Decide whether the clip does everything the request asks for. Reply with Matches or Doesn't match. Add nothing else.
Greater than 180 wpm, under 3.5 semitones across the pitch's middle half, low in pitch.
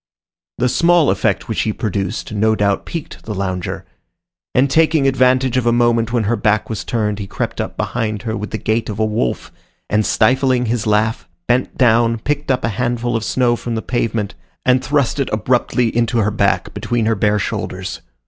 Matches